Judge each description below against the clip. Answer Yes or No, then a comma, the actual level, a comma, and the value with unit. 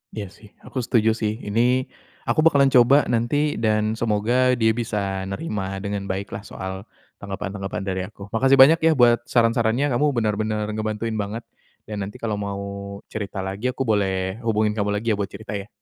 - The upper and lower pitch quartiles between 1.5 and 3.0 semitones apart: Yes, narrow, 2.5 semitones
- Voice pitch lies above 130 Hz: No, low, 110 Hz